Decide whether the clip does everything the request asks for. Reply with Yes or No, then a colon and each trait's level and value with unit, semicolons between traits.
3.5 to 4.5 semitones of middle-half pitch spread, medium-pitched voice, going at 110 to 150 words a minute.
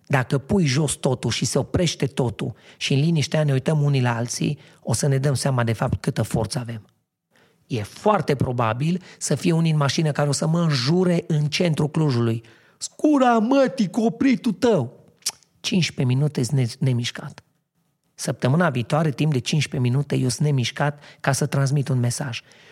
No: average, 4.0 semitones; medium, 145 Hz; fast, 170 wpm